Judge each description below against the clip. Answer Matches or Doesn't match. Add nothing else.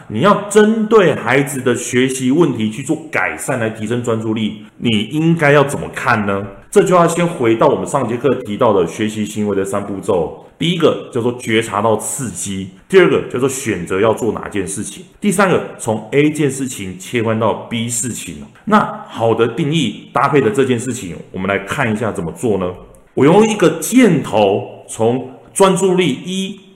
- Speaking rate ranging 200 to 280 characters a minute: Matches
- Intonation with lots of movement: Matches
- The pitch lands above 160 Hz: Doesn't match